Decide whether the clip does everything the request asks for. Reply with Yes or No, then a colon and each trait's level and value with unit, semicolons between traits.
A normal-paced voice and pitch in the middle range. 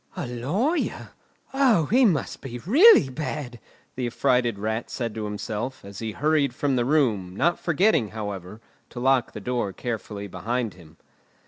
No: average, 155 wpm; low, 125 Hz